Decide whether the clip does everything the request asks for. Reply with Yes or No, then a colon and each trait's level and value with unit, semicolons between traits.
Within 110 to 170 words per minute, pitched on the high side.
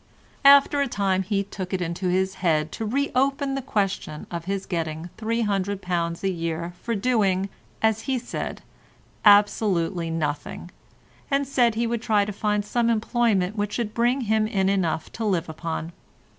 Yes: average, 160 wpm; high, 200 Hz